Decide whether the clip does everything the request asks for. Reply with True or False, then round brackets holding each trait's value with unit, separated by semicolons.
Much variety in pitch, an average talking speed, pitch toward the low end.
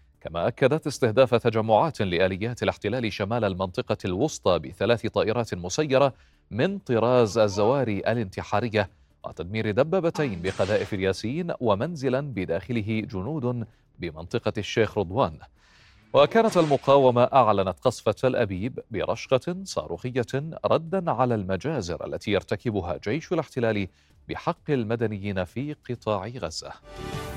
False (4.6 semitones; 100 wpm; 115 Hz)